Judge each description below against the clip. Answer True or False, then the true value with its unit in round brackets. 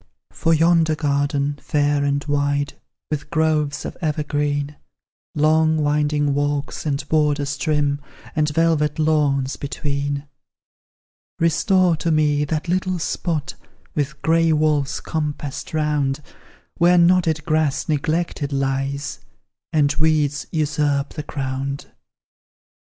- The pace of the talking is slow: True (105 wpm)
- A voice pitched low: False (150 Hz)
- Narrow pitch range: True (1.7 semitones)